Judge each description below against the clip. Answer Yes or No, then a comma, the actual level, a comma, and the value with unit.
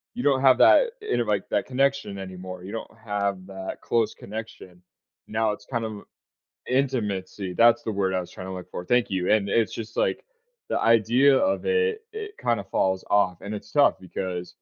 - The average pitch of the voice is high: No, low, 105 Hz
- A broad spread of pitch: No, average, 5.0 semitones